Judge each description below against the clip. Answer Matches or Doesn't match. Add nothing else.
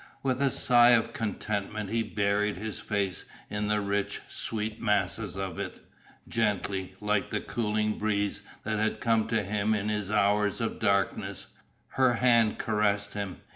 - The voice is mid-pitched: Doesn't match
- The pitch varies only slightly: Matches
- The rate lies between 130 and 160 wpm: Matches